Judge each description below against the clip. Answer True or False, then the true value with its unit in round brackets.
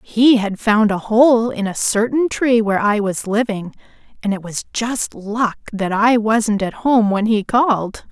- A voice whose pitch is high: True (220 Hz)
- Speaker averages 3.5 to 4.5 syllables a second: True (4.1 syllables/s)